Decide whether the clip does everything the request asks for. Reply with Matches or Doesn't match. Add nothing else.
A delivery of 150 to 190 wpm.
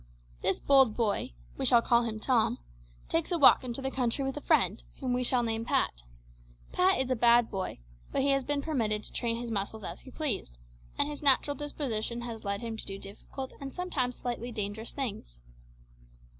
Doesn't match